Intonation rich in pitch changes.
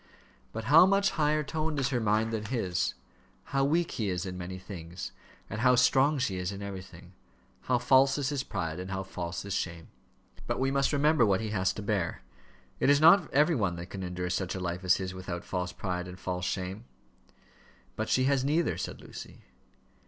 Yes: wide, 7.0 semitones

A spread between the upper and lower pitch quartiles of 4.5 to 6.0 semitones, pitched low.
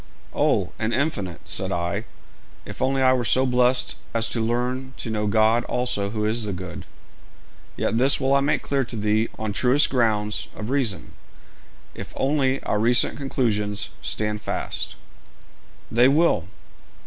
No: average, 3.7 semitones; low, 115 Hz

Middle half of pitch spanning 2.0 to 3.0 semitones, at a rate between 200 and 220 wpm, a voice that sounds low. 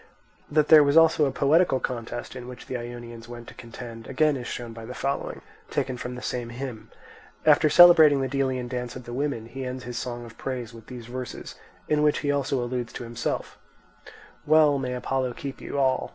Yes: average, 2.7 semitones; fast, 205 wpm; low, 125 Hz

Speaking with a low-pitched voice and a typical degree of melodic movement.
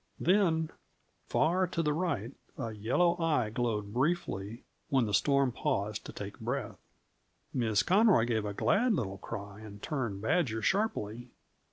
No: low, 125 Hz; wide, 7.6 semitones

